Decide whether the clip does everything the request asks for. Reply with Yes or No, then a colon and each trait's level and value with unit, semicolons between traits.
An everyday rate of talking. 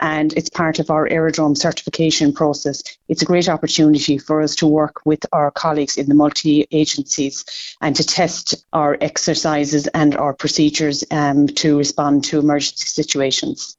Yes: average, 160 wpm